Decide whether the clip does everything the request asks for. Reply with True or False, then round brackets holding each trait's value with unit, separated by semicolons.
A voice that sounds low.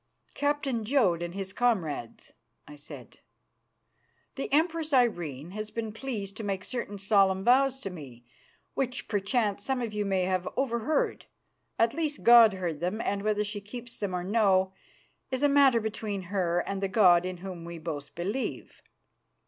False (205 Hz)